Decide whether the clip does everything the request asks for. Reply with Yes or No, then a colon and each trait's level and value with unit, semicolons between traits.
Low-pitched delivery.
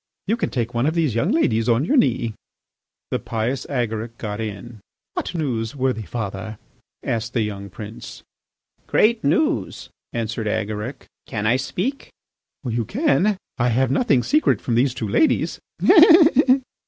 Yes: low, 120 Hz